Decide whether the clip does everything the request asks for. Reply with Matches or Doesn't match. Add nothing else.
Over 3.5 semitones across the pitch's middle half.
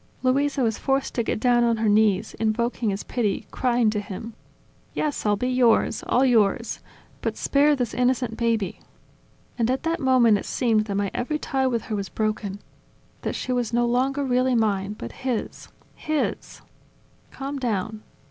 Doesn't match